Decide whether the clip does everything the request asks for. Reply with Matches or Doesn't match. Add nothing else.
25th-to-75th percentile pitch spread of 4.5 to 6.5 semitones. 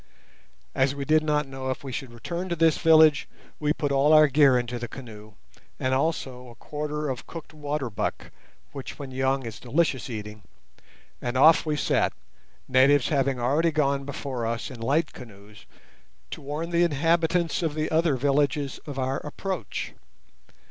Doesn't match